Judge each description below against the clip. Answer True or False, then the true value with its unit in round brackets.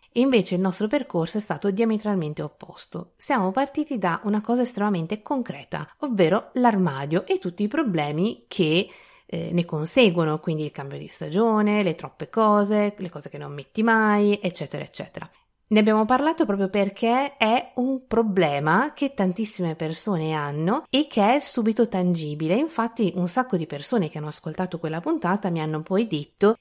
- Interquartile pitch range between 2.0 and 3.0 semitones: False (5.4 semitones)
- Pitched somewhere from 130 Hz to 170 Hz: False (200 Hz)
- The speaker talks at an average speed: True (160 wpm)